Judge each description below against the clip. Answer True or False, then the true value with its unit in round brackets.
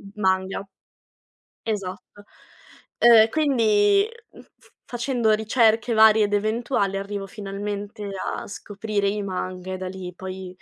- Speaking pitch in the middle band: False (205 Hz)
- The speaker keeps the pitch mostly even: True (2.3 semitones)